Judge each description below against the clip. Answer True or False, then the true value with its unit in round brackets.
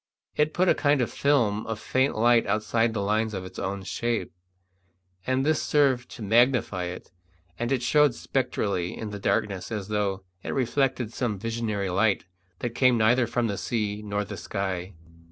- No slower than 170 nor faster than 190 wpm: True (175 wpm)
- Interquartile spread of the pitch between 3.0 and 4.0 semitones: True (3.7 semitones)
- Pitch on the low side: True (110 Hz)